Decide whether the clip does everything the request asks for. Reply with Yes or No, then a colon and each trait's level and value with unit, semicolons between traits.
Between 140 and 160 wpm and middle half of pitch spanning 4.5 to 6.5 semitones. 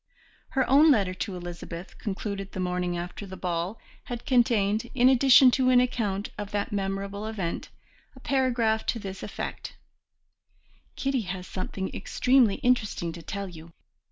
Yes: average, 150 wpm; average, 4.9 semitones